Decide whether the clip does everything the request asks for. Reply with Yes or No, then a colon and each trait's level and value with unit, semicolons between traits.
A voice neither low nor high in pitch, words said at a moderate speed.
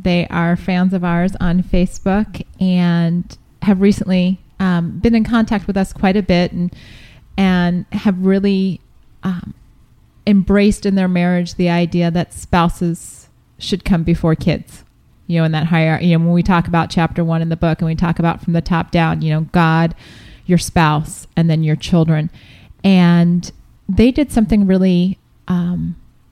Yes: medium, 175 Hz; average, 170 wpm